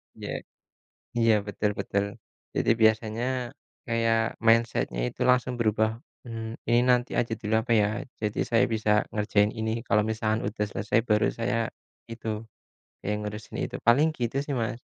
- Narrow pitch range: Yes, narrow, 1.6 semitones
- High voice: No, low, 110 Hz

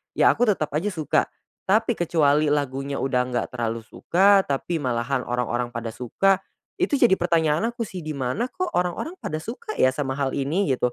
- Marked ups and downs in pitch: Yes, wide, 6.9 semitones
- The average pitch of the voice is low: No, medium, 150 Hz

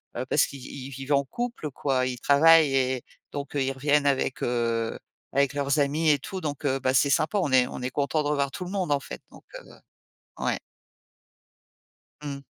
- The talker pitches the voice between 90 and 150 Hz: Yes, medium, 140 Hz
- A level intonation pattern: Yes, narrow, 2.2 semitones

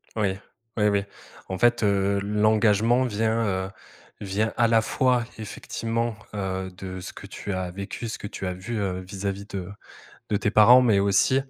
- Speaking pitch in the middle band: No, low, 105 Hz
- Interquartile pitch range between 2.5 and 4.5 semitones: Yes, average, 2.8 semitones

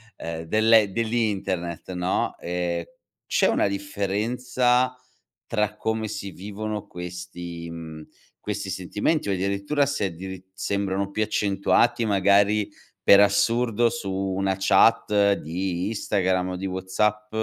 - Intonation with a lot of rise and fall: No, narrow, 2.6 semitones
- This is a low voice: Yes, low, 100 Hz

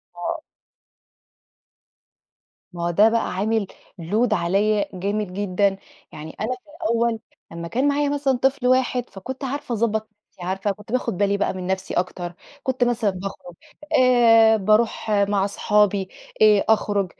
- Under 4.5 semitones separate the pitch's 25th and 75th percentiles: Yes, average, 3.7 semitones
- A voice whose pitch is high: Yes, high, 210 Hz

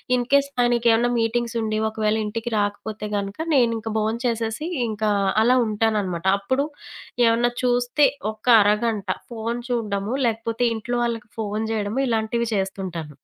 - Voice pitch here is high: Yes, high, 225 Hz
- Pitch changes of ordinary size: No, narrow, 2.1 semitones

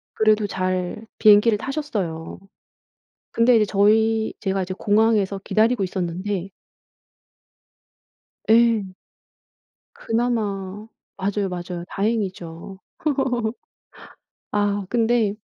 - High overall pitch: Yes, high, 205 Hz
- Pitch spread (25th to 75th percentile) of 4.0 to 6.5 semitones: No, average, 2.8 semitones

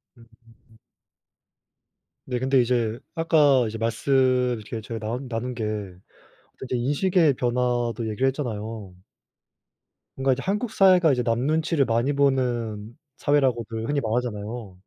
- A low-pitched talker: Yes, low, 120 Hz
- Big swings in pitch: No, average, 3.4 semitones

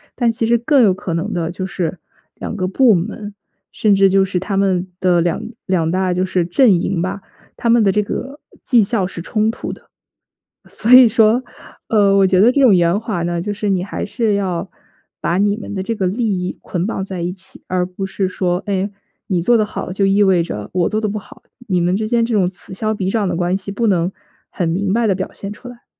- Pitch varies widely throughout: No, average, 2.9 semitones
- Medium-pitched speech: No, high, 195 Hz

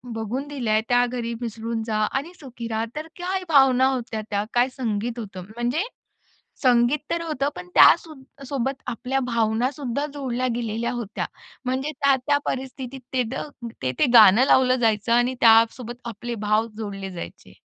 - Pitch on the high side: Yes, high, 245 Hz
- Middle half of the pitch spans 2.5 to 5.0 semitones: Yes, average, 3.0 semitones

